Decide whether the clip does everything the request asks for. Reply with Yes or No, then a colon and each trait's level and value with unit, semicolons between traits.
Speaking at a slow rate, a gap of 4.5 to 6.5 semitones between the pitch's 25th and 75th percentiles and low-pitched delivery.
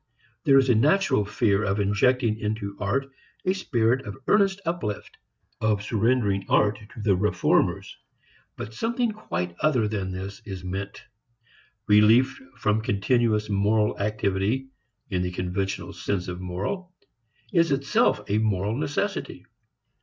Yes: slow, 130 wpm; average, 5.1 semitones; low, 105 Hz